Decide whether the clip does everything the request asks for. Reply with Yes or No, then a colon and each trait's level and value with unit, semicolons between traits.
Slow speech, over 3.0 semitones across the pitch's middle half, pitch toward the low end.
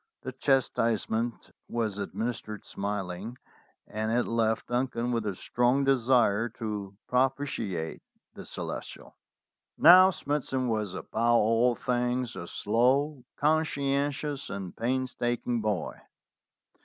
Yes: slow, 110 wpm; average, 3.4 semitones; low, 120 Hz